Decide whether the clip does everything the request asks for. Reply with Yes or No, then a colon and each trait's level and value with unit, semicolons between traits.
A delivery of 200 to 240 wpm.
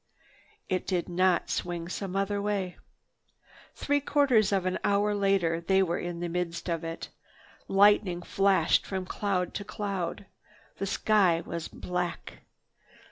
No: slow, 135 wpm